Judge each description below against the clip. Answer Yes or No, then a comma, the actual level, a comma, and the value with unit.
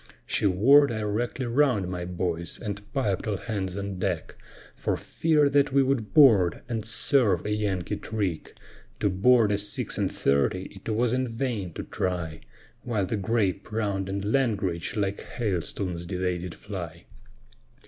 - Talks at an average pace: Yes, average, 155 wpm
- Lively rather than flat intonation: No, average, 4.2 semitones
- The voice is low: Yes, low, 100 Hz